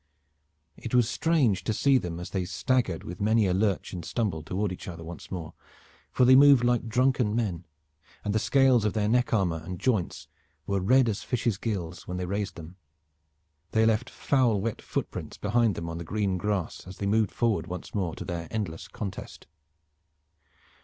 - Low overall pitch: Yes, low, 105 Hz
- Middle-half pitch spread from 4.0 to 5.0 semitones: Yes, average, 4.6 semitones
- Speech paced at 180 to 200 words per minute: Yes, average, 190 wpm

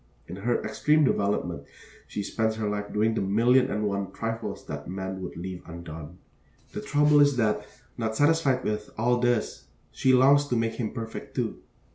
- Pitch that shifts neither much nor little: Yes, average, 4.2 semitones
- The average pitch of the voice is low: Yes, low, 110 Hz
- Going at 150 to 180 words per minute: Yes, average, 175 wpm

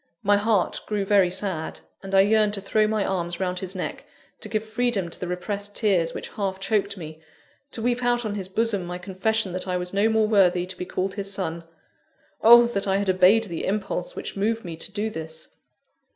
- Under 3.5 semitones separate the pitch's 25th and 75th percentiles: Yes, average, 2.9 semitones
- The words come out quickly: Yes, fast, 215 wpm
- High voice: Yes, high, 195 Hz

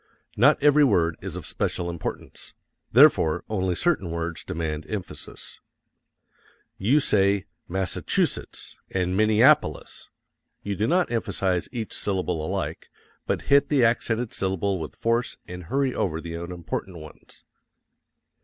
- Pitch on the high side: No, very low, 95 Hz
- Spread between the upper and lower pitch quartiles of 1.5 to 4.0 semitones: No, average, 5.1 semitones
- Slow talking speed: Yes, slow, 125 wpm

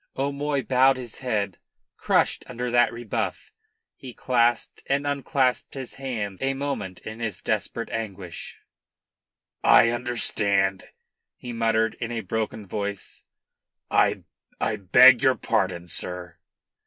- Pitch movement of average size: Yes, average, 4.1 semitones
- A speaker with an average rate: No, slow, 120 wpm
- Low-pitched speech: Yes, low, 115 Hz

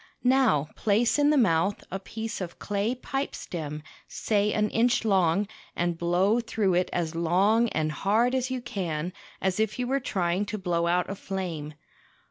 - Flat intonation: No, average, 4.7 semitones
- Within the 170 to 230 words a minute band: Yes, average, 175 wpm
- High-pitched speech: Yes, high, 195 Hz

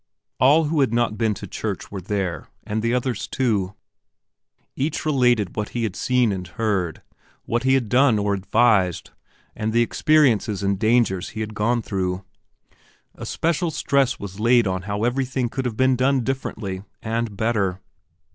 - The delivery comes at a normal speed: Yes, average, 165 wpm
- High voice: No, low, 115 Hz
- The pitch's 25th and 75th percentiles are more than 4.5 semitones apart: No, average, 4.1 semitones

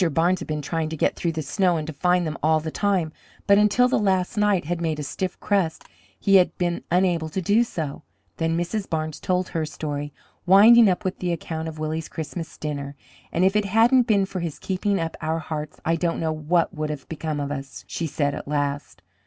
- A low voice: No, medium, 165 Hz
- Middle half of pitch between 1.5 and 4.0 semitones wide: Yes, average, 3.4 semitones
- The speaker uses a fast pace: Yes, fast, 225 wpm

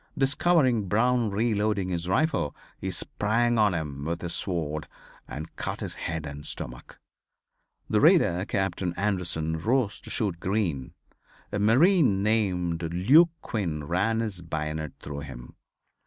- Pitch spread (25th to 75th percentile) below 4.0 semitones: No, wide, 5.5 semitones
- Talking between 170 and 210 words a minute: No, slow, 135 wpm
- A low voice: Yes, very low, 95 Hz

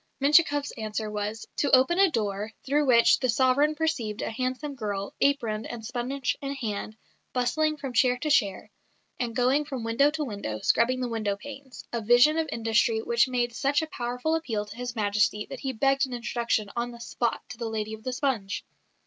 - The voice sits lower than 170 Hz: No, high, 245 Hz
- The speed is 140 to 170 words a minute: No, average, 195 wpm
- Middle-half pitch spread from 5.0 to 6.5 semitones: No, average, 3.8 semitones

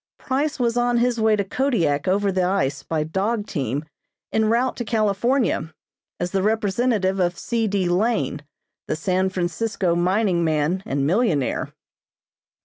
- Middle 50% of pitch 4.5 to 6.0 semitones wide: Yes, average, 4.9 semitones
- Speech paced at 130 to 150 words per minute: Yes, average, 145 wpm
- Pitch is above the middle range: Yes, high, 195 Hz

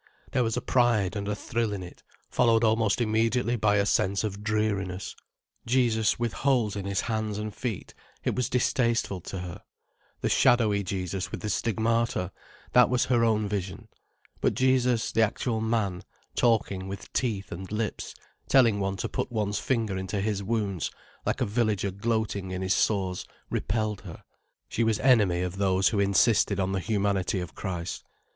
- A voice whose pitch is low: Yes, low, 105 Hz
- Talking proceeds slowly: No, average, 170 wpm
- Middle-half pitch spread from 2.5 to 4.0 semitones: Yes, average, 2.9 semitones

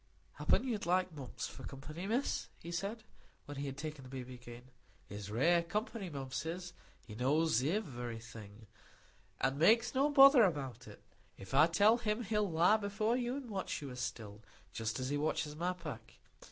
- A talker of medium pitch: Yes, medium, 160 Hz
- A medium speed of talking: Yes, average, 175 wpm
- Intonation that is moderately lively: No, wide, 8.1 semitones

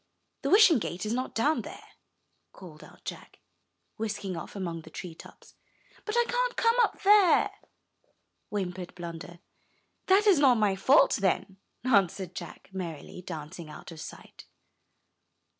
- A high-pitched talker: Yes, high, 195 Hz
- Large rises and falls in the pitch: Yes, wide, 8.9 semitones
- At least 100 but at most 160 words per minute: Yes, average, 140 wpm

